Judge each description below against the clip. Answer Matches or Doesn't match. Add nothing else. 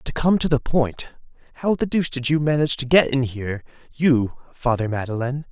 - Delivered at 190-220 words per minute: Matches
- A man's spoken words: Matches